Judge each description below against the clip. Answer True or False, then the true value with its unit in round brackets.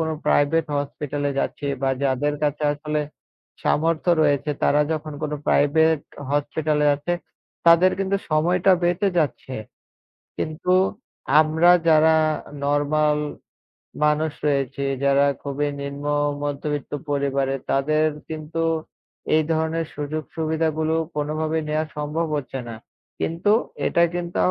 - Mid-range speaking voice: True (155 Hz)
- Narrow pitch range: True (1.8 semitones)